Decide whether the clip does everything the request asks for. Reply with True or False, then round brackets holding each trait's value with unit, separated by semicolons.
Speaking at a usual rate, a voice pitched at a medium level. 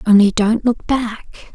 False (155 wpm; 220 Hz)